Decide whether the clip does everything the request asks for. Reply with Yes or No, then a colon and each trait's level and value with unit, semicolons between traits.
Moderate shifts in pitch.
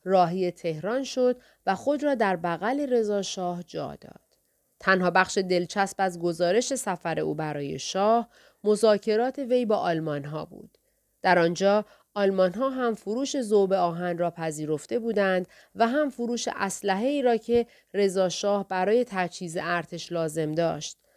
Yes: average, 4.9 semitones